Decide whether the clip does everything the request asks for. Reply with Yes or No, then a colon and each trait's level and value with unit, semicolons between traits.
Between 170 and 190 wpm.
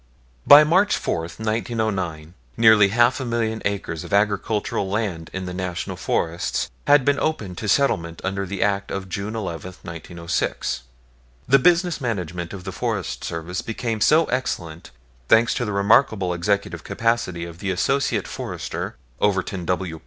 No: average, 150 wpm